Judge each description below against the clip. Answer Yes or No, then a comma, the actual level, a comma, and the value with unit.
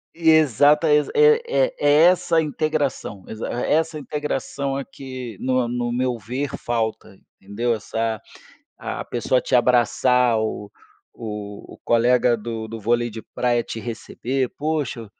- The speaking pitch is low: Yes, low, 125 Hz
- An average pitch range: Yes, average, 4.2 semitones